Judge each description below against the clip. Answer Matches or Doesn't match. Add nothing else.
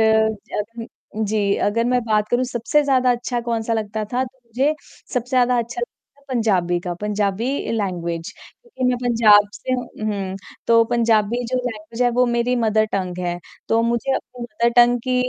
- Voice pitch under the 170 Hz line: Doesn't match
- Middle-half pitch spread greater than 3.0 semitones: Doesn't match